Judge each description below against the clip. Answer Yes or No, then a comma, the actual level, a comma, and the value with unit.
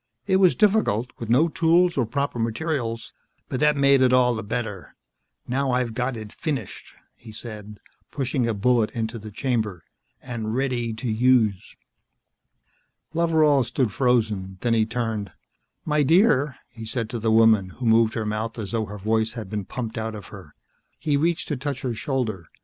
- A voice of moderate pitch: No, low, 120 Hz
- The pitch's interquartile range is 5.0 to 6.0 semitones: No, average, 3.5 semitones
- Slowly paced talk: No, average, 175 wpm